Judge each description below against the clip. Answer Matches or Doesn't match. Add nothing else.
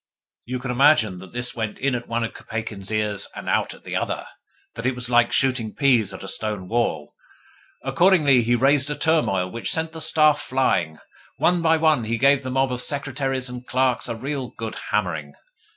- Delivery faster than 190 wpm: Matches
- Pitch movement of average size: Matches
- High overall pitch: Doesn't match